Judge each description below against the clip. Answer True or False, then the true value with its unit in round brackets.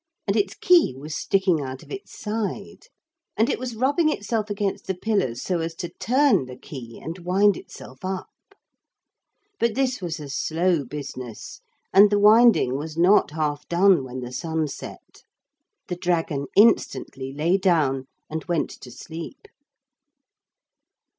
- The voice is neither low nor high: True (175 Hz)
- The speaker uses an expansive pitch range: True (6.1 semitones)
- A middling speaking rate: True (150 wpm)